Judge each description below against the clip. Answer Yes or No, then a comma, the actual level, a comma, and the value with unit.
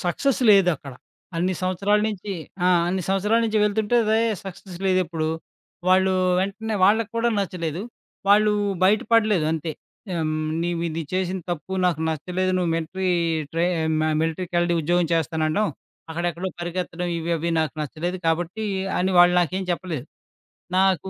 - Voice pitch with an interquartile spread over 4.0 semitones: No, average, 2.8 semitones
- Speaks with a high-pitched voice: No, medium, 180 Hz